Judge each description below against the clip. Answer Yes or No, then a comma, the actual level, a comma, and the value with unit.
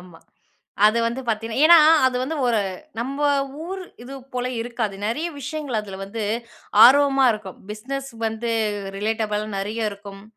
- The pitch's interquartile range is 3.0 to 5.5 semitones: Yes, average, 4.2 semitones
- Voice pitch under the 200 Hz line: No, high, 230 Hz